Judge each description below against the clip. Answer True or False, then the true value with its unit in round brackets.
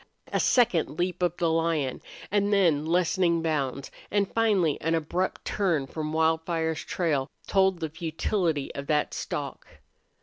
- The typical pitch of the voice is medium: True (165 Hz)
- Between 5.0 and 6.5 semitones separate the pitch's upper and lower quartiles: False (2.9 semitones)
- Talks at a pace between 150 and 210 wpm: False (140 wpm)